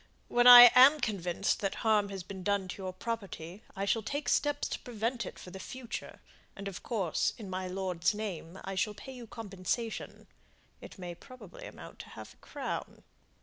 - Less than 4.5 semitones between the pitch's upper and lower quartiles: Yes, average, 4.0 semitones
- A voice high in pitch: Yes, high, 200 Hz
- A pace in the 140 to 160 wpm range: No, average, 190 wpm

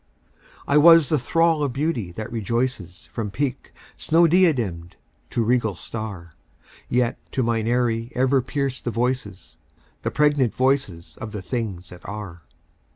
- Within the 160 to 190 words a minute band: No, average, 145 wpm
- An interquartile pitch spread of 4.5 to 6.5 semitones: Yes, average, 4.9 semitones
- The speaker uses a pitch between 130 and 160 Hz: No, low, 120 Hz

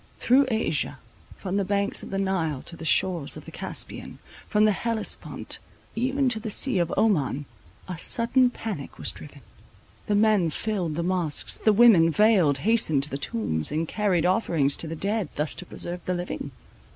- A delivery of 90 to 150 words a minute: No, average, 180 wpm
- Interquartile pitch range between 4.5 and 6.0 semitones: Yes, average, 5.2 semitones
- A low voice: No, medium, 185 Hz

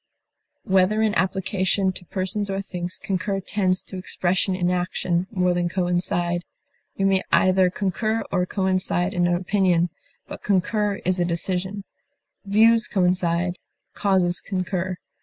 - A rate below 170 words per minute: Yes, slow, 135 wpm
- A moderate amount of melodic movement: No, narrow, 1.6 semitones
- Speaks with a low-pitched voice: No, medium, 185 Hz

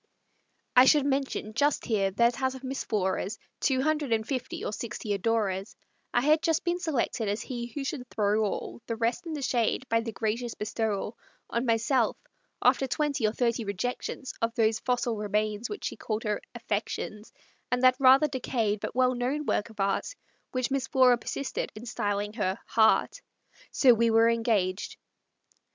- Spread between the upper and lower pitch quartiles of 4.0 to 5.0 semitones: No, average, 3.5 semitones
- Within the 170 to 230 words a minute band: Yes, average, 175 wpm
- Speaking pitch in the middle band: No, high, 235 Hz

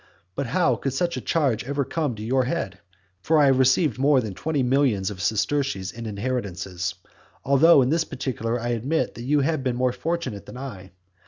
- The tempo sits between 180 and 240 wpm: Yes, average, 195 wpm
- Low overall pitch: Yes, low, 130 Hz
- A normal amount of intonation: Yes, average, 4.5 semitones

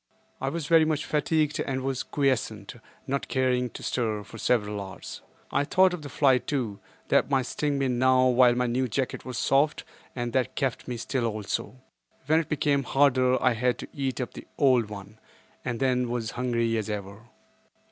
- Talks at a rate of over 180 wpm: Yes, average, 190 wpm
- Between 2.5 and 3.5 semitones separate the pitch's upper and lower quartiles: Yes, average, 2.9 semitones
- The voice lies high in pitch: No, low, 130 Hz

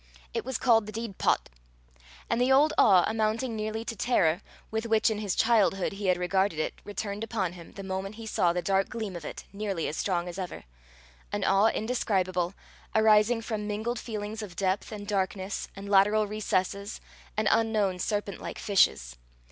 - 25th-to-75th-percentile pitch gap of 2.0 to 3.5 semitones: Yes, average, 2.7 semitones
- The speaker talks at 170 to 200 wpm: Yes, average, 180 wpm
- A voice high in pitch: Yes, high, 205 Hz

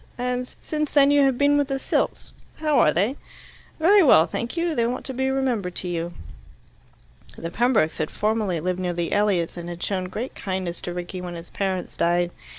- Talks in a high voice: Yes, high, 205 Hz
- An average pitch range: No, wide, 7.2 semitones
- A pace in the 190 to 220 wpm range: Yes, average, 200 wpm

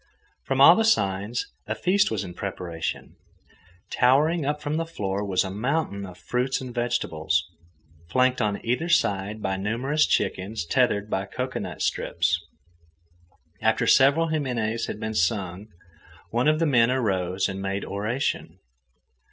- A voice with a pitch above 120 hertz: No, low, 110 Hz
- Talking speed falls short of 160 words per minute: Yes, average, 145 wpm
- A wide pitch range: Yes, wide, 5.7 semitones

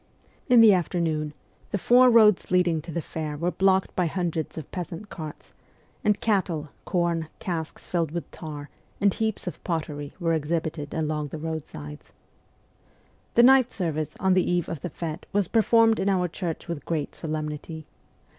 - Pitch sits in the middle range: Yes, medium, 170 Hz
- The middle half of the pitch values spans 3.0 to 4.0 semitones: Yes, average, 3.5 semitones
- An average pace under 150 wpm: No, average, 165 wpm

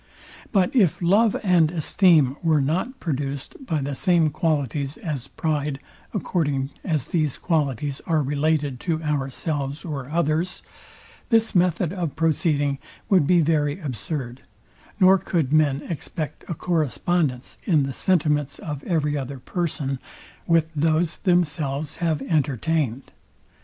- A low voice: No, medium, 155 Hz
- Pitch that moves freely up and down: No, average, 3.3 semitones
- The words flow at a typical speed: No, slow, 125 wpm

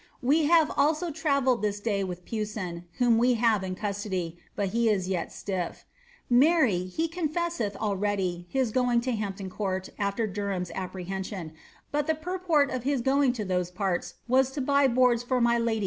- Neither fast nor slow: Yes, average, 170 wpm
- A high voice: Yes, high, 225 Hz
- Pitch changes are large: Yes, wide, 5.7 semitones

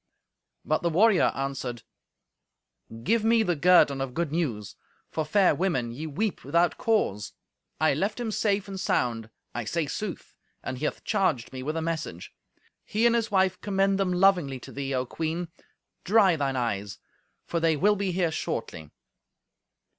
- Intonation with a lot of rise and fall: Yes, wide, 6.5 semitones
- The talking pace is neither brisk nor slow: Yes, average, 160 wpm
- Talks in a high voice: No, medium, 165 Hz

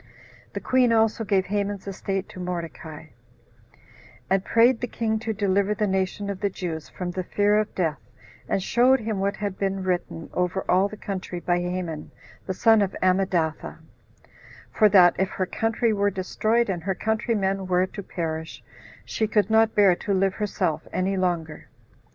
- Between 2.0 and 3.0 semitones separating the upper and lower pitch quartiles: Yes, average, 2.7 semitones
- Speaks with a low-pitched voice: No, high, 195 Hz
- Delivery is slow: No, average, 170 wpm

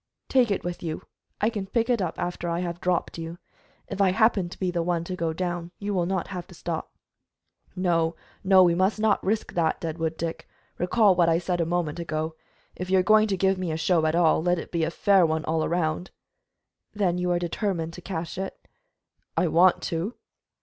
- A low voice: No, medium, 175 Hz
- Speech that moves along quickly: Yes, fast, 220 wpm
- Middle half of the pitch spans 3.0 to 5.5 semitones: No, narrow, 2.4 semitones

